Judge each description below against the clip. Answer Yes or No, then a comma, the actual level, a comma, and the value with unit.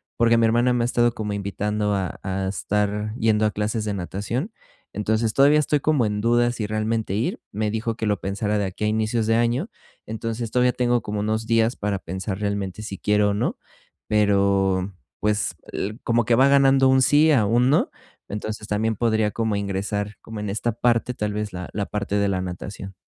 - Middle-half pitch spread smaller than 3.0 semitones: Yes, narrow, 2.4 semitones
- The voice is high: No, low, 105 Hz